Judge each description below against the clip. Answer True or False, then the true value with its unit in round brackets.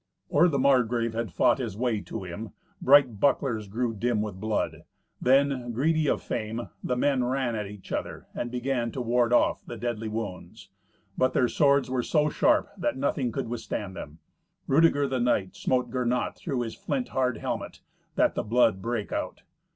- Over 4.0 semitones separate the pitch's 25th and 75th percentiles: False (3.2 semitones)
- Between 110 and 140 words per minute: False (180 wpm)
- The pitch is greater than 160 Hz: False (120 Hz)